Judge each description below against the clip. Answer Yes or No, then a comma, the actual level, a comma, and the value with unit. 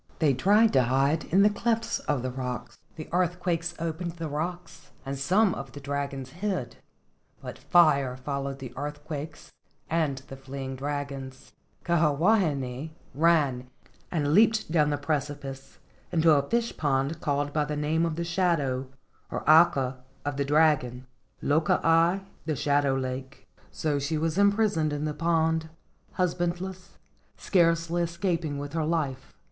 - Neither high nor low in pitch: Yes, medium, 150 Hz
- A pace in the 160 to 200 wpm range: No, average, 150 wpm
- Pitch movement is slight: No, average, 3.5 semitones